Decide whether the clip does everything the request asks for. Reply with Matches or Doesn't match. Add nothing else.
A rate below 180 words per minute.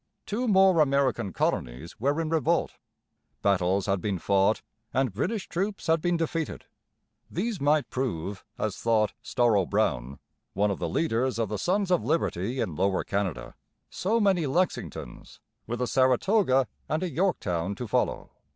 Matches